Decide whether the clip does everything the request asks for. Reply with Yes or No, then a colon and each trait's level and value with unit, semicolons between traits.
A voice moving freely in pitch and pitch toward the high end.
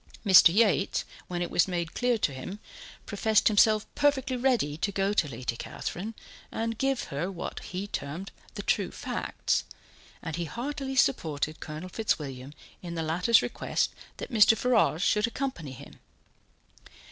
Yes: wide, 6.2 semitones; high, 195 Hz